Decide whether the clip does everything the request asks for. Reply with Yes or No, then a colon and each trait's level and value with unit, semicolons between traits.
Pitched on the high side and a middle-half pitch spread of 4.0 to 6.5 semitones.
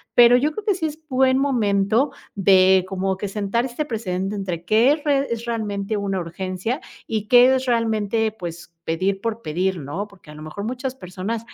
Yes: high, 210 Hz; average, 4.5 semitones